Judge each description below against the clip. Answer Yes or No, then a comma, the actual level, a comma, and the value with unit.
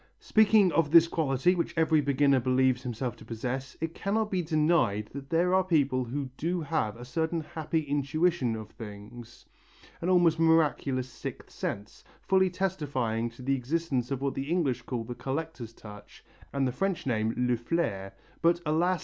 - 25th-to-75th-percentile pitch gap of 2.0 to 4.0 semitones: No, average, 5.3 semitones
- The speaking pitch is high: No, medium, 140 Hz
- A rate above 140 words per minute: Yes, average, 170 wpm